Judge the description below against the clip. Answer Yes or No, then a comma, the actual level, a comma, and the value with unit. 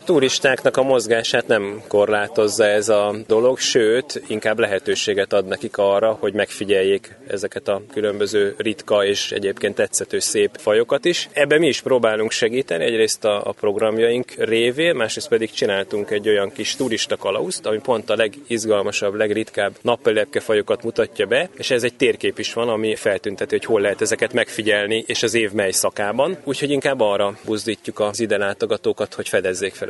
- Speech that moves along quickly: Yes, fast, 160 wpm